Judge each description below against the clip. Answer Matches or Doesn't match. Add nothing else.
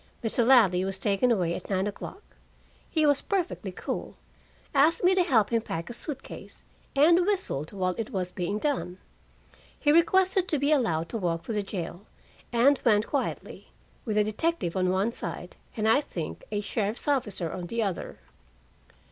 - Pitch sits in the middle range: Doesn't match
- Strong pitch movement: Matches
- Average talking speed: Matches